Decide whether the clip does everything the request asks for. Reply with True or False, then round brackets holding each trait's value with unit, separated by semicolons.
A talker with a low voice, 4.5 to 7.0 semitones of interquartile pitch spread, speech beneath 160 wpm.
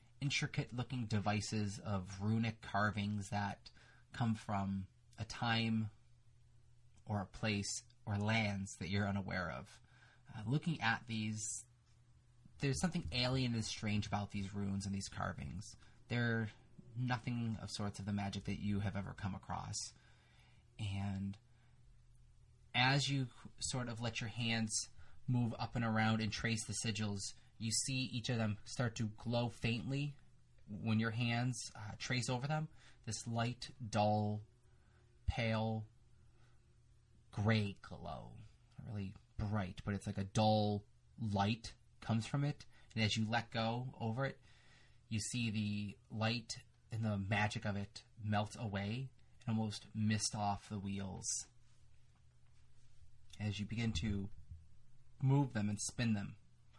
False (110 Hz; 2.5 semitones; 140 wpm)